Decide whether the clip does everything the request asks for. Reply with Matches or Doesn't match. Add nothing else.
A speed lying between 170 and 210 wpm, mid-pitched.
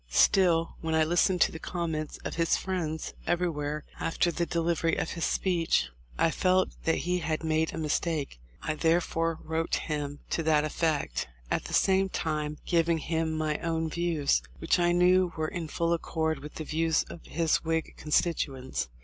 Matches